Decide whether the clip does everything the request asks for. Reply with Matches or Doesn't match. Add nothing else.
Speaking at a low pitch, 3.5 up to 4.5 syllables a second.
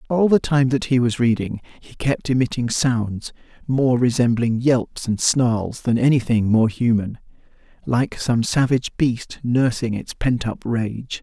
Matches